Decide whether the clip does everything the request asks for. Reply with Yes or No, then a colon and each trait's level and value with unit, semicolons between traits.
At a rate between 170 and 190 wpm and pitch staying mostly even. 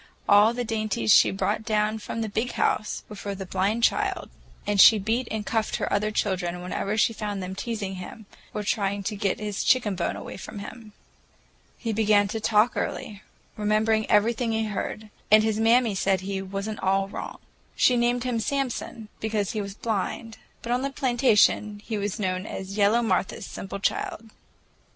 Yes: average, 185 wpm; narrow, 2.0 semitones